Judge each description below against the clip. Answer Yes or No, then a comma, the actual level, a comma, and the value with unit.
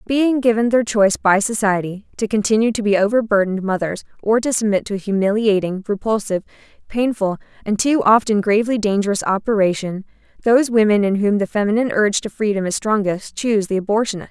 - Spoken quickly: No, average, 165 wpm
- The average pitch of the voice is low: No, high, 210 Hz